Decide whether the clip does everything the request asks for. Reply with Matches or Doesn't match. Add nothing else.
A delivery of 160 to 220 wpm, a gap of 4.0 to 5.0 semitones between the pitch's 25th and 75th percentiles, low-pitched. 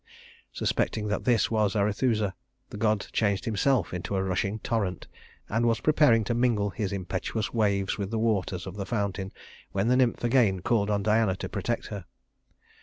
Doesn't match